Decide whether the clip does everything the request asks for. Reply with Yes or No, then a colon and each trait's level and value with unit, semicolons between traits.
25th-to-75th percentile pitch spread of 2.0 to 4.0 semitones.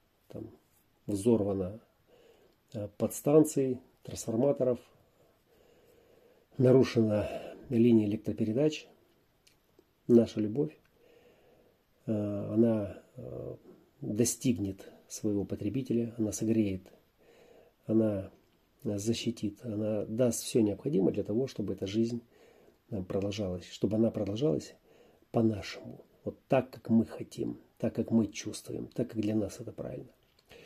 Yes: average, 3.0 semitones